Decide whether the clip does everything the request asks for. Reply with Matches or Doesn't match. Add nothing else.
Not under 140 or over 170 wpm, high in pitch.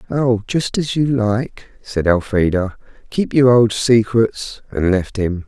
Doesn't match